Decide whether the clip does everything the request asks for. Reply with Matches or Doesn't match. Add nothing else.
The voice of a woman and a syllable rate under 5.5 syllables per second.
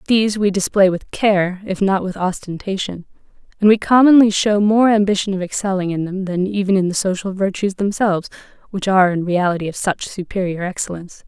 Doesn't match